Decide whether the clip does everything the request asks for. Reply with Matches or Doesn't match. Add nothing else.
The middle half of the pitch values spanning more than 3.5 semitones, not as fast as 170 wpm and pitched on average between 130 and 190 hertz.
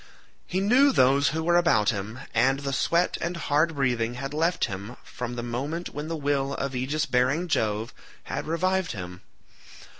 Doesn't match